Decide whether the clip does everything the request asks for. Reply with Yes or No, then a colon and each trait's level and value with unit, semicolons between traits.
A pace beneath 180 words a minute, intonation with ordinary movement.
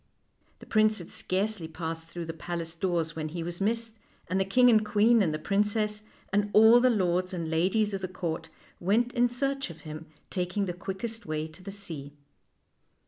No: average, 195 wpm; average, 4.6 semitones